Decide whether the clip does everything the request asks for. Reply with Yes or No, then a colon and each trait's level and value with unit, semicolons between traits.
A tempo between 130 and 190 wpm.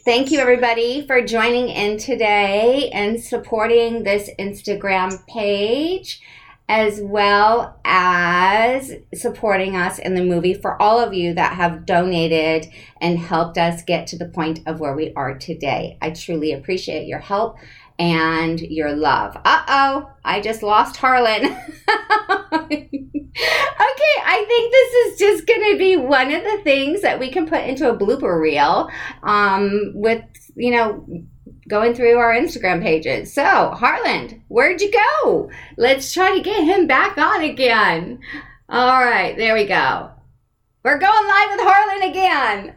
Yes: average, 150 wpm